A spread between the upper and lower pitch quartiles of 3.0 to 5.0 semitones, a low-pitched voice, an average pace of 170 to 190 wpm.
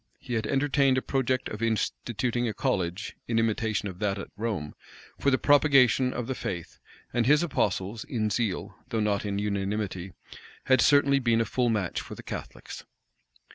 Yes: average, 4.1 semitones; low, 115 Hz; average, 175 wpm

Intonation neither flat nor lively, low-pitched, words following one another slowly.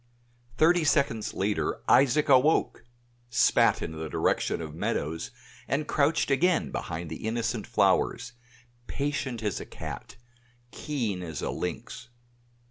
No: wide, 7.3 semitones; low, 120 Hz; slow, 125 wpm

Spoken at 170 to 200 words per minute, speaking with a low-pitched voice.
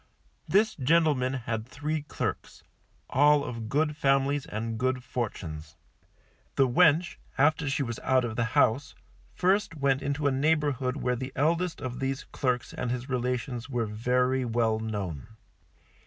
No: average, 145 wpm; low, 130 Hz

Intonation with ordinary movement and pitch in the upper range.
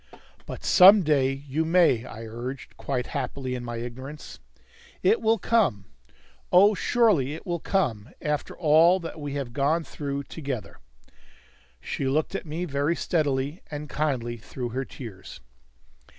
No: average, 4.5 semitones; medium, 140 Hz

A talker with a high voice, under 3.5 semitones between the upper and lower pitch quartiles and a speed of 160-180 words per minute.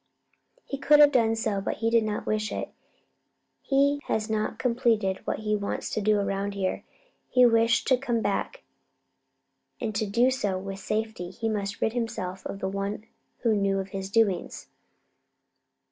Yes: high, 215 Hz; average, 2.7 semitones; average, 170 wpm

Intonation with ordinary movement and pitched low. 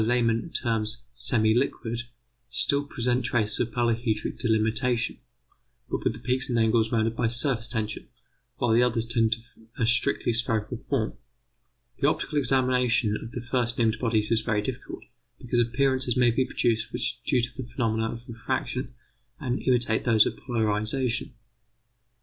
No: narrow, 1.8 semitones; low, 120 Hz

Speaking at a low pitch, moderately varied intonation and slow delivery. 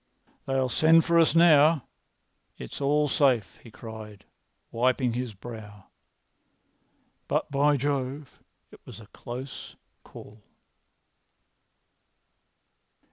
Yes: low, 130 Hz; average, 4.5 semitones; slow, 95 wpm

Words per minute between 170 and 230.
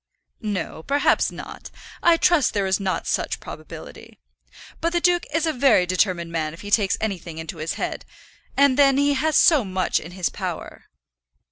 Yes: average, 175 wpm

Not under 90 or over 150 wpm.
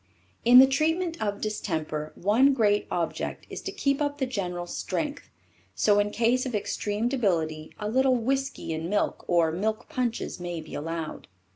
No: average, 165 wpm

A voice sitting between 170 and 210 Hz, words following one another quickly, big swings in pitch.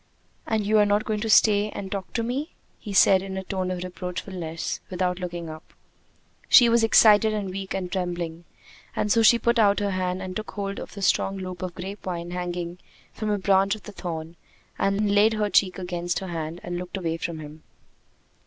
No: high, 190 Hz; fast, 210 wpm; average, 2.8 semitones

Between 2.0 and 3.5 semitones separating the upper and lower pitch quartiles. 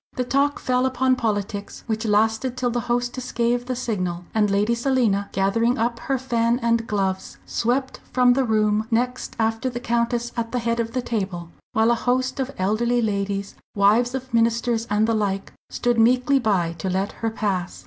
Yes: average, 2.8 semitones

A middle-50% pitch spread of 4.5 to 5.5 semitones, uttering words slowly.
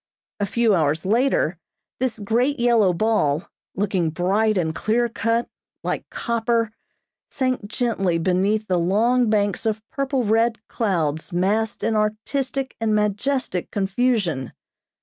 No: average, 4.0 semitones; slow, 125 wpm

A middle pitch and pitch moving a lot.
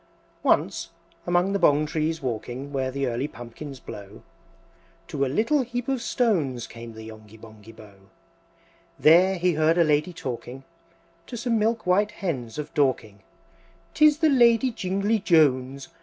Yes: medium, 150 Hz; wide, 8.3 semitones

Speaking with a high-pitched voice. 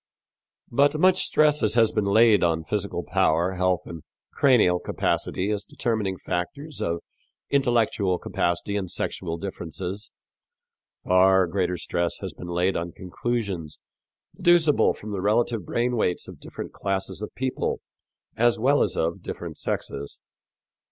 No: low, 100 Hz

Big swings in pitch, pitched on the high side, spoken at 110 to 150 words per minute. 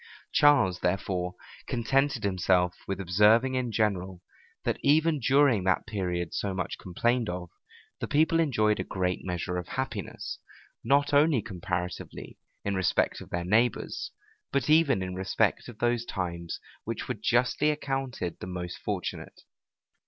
No: wide, 6.6 semitones; low, 105 Hz; average, 140 wpm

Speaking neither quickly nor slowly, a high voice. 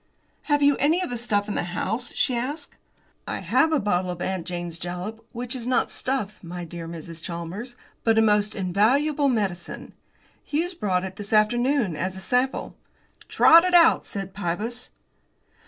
Yes: average, 170 wpm; high, 210 Hz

